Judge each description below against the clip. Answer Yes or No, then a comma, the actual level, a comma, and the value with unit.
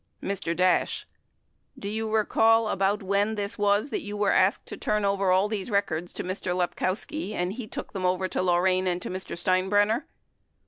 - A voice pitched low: No, high, 200 Hz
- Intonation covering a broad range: No, narrow, 2.4 semitones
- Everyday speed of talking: Yes, average, 180 wpm